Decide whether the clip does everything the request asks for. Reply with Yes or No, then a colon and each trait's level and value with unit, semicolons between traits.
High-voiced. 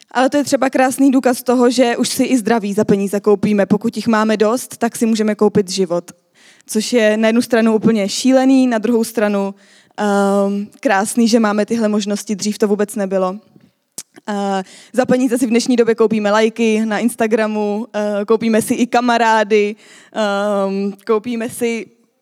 Yes: high, 220 Hz